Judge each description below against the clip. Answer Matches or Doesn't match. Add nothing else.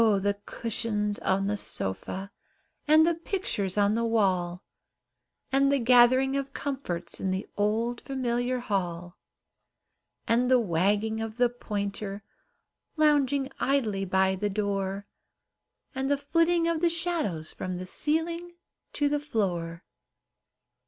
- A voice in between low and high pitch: Doesn't match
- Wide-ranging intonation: Matches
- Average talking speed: Doesn't match